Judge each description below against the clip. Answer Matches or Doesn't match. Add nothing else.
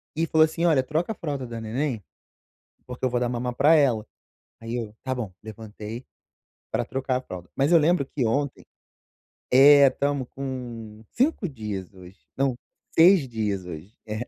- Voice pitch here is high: Doesn't match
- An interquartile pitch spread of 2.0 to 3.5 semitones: Doesn't match